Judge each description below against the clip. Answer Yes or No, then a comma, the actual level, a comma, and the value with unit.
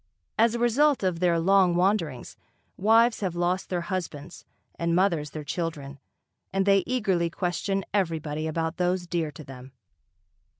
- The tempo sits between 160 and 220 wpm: No, average, 145 wpm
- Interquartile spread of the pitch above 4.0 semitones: No, average, 3.2 semitones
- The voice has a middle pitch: Yes, medium, 175 Hz